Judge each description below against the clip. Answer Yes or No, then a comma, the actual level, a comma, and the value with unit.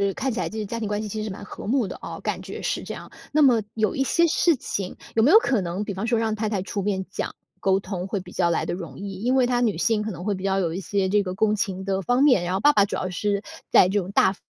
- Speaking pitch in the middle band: No, high, 205 Hz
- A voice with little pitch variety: No, average, 3.1 semitones